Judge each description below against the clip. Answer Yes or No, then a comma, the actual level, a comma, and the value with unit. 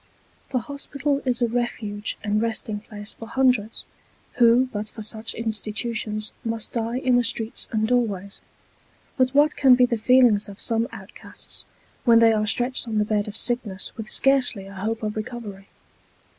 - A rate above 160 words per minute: Yes, average, 170 wpm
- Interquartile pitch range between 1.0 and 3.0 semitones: Yes, average, 2.7 semitones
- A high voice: Yes, high, 225 Hz